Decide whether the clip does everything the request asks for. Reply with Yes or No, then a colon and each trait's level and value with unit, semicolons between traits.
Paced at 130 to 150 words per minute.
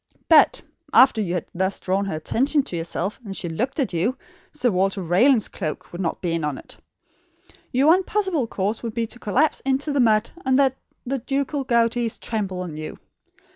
No: average, 190 wpm